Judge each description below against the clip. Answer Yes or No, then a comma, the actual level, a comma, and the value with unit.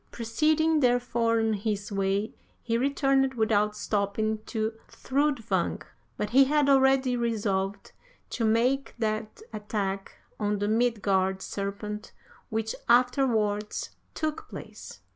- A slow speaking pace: Yes, slow, 110 wpm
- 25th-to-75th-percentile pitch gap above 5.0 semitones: No, average, 3.6 semitones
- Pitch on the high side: Yes, high, 225 Hz